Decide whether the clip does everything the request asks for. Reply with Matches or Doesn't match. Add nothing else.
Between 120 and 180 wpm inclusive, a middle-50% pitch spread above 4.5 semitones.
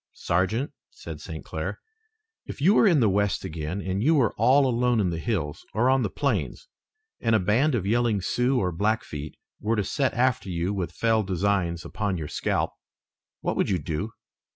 Doesn't match